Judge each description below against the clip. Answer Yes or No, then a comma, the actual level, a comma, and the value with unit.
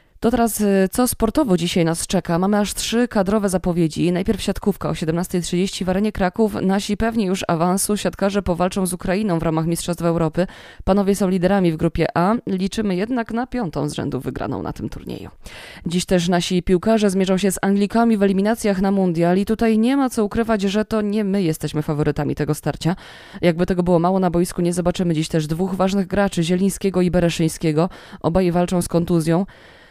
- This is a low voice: No, medium, 185 Hz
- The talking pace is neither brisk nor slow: No, fast, 185 wpm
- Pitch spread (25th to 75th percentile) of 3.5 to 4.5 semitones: No, average, 3.0 semitones